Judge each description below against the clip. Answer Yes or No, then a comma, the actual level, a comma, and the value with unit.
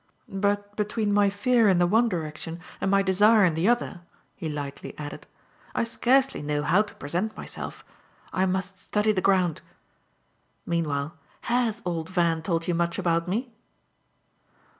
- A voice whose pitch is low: No, high, 190 Hz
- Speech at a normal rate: Yes, average, 155 wpm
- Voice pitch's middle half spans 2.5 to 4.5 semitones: Yes, average, 3.9 semitones